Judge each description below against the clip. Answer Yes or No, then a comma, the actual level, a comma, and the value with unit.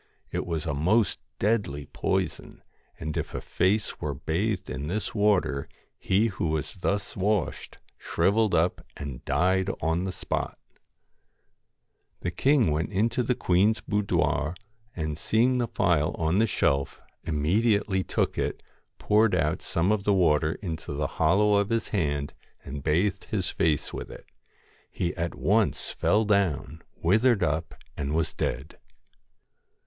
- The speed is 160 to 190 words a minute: No, average, 150 wpm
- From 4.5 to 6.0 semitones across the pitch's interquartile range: Yes, average, 5.0 semitones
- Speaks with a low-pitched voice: Yes, very low, 90 Hz